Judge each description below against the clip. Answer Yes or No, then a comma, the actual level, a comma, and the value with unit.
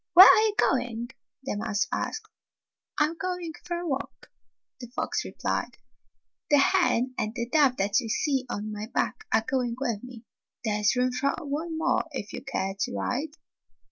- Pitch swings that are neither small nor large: No, wide, 5.7 semitones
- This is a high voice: Yes, very high, 255 Hz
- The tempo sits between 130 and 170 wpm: No, average, 180 wpm